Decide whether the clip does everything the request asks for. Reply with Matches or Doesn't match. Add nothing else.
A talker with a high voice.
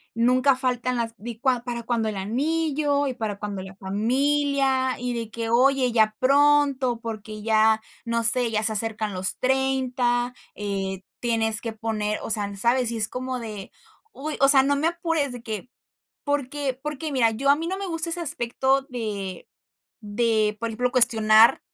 Matches